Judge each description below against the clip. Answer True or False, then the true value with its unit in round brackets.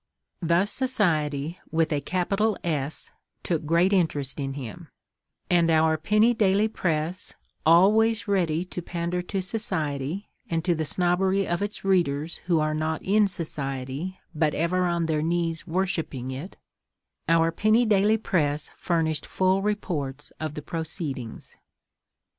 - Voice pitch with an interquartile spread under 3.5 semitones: False (3.8 semitones)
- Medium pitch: True (170 Hz)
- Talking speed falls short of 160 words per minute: True (135 wpm)